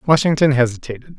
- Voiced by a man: Yes, male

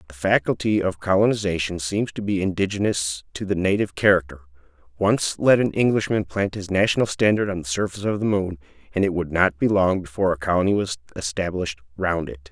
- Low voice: Yes, very low, 95 Hz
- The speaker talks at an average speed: Yes, average, 185 wpm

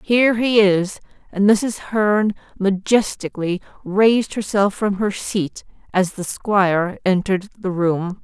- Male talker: No, female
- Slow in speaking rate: Yes, slow, 130 wpm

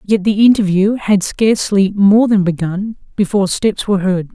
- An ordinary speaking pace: Yes, average, 165 wpm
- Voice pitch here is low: No, high, 200 Hz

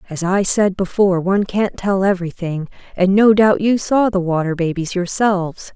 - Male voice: No, female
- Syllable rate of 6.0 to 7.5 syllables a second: No, 5.1 syllables/s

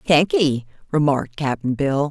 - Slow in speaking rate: Yes, slow, 115 wpm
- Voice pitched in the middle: Yes, medium, 150 Hz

